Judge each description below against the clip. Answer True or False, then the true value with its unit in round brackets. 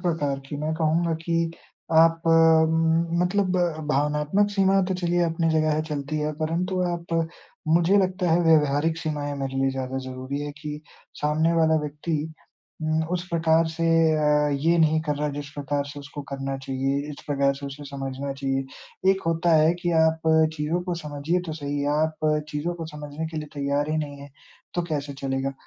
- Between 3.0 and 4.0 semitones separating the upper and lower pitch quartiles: False (2.5 semitones)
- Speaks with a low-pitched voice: False (155 Hz)